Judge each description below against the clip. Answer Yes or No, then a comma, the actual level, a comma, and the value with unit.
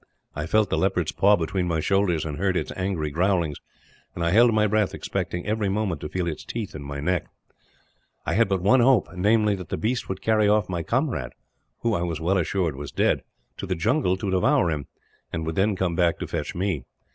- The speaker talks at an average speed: No, fast, 220 wpm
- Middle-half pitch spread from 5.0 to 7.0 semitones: No, average, 4.0 semitones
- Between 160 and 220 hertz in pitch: No, very low, 95 Hz